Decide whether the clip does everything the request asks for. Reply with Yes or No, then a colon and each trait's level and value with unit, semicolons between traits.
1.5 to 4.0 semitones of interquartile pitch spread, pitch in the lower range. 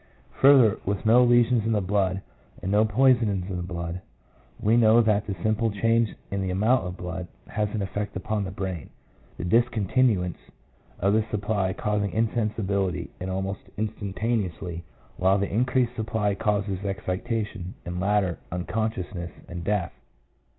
Yes: average, 3.0 semitones; low, 105 Hz